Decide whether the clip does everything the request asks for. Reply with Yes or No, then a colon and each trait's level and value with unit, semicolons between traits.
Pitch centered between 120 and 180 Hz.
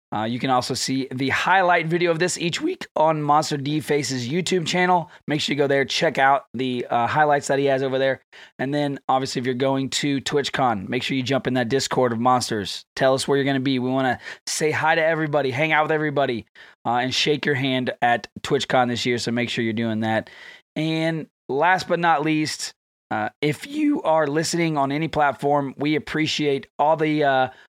Yes: medium, 140 Hz